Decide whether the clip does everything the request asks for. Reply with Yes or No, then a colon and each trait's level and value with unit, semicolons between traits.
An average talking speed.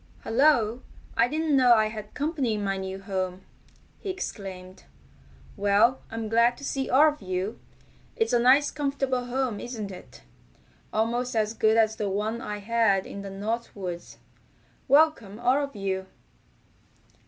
Yes: average, 155 wpm